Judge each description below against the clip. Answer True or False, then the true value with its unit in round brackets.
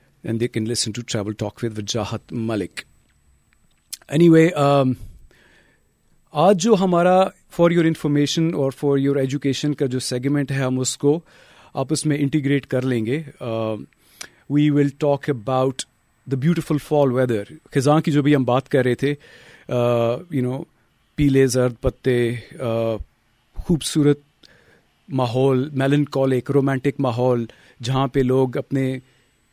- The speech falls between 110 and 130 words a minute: True (125 wpm)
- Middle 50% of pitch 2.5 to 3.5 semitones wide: True (3.0 semitones)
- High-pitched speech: False (135 Hz)